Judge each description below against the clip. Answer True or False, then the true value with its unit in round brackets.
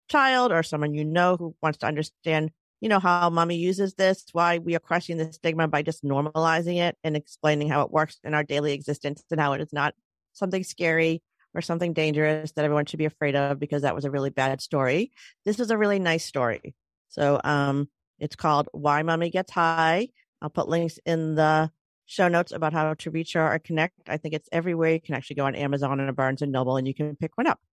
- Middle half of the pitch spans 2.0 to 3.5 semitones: True (2.4 semitones)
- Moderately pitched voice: True (160 Hz)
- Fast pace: True (225 wpm)